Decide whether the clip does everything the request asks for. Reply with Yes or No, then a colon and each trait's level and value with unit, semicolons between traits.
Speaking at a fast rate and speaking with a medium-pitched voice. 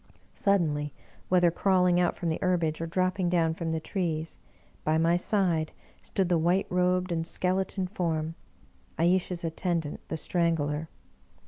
No: average, 150 wpm; medium, 170 Hz